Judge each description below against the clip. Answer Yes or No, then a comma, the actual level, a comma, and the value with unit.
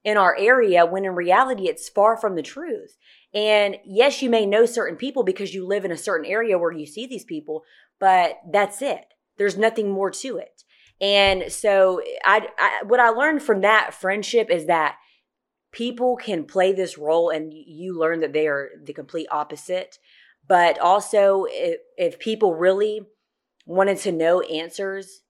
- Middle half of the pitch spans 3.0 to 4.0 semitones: No, average, 4.4 semitones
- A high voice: Yes, high, 195 Hz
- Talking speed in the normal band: Yes, average, 175 wpm